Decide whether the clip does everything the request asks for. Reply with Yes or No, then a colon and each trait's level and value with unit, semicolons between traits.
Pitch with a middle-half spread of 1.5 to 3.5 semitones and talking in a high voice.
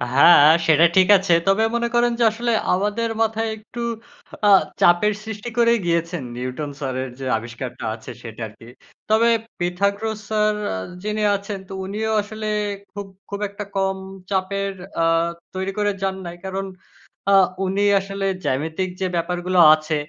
No: average, 3.9 semitones; high, 195 Hz